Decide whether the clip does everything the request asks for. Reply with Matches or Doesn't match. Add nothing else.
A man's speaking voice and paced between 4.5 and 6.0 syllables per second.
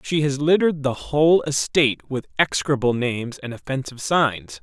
Matches